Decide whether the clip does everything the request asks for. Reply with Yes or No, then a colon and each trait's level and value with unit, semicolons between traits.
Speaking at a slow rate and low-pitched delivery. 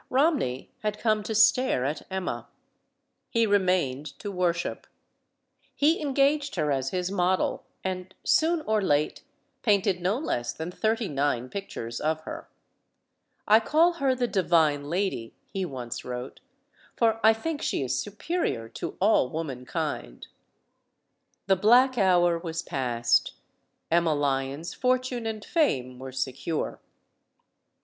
No: slow, 130 wpm; medium, 185 Hz